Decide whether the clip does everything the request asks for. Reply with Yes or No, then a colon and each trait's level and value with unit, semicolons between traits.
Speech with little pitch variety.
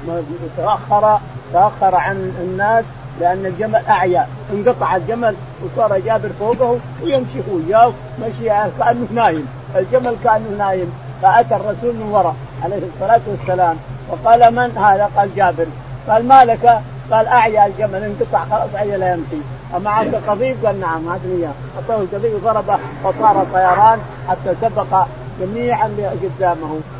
No: average, 5.1 semitones